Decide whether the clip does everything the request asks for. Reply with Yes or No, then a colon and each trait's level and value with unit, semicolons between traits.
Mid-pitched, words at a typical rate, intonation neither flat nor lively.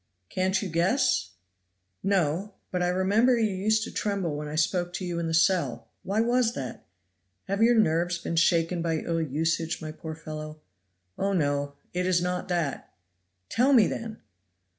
Yes: medium, 180 Hz; average, 170 wpm; average, 3.7 semitones